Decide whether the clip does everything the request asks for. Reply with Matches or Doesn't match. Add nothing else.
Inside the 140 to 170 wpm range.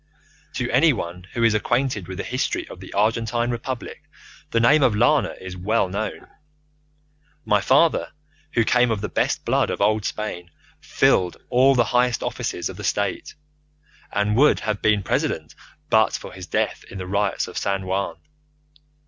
Matches